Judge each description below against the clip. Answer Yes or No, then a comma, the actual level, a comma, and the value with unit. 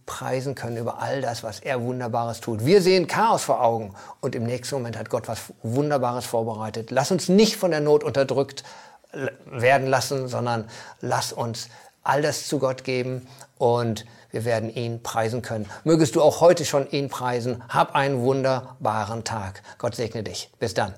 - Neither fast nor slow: Yes, average, 175 wpm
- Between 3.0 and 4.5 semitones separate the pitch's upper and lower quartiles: Yes, average, 3.3 semitones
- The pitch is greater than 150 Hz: No, low, 125 Hz